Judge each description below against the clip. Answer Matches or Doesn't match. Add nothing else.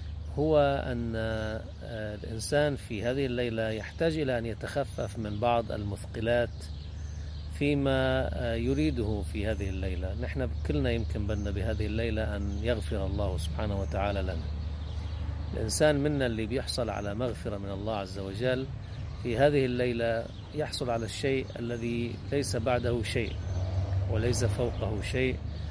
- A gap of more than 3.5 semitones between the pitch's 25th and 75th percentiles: Matches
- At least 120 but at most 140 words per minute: Matches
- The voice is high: Doesn't match